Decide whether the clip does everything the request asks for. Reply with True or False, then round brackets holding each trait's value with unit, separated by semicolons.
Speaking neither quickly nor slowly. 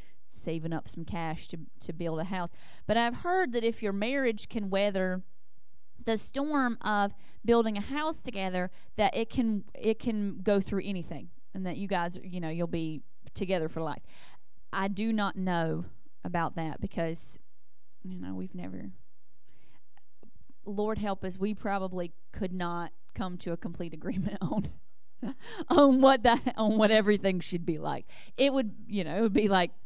True (170 wpm)